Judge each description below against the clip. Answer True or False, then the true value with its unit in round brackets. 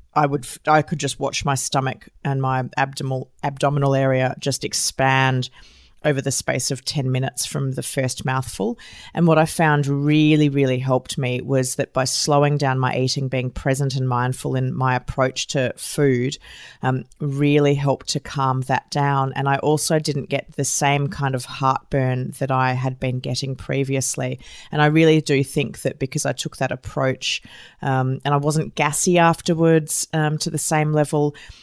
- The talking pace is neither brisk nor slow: True (180 wpm)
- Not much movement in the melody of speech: True (2.2 semitones)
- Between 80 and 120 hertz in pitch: False (135 Hz)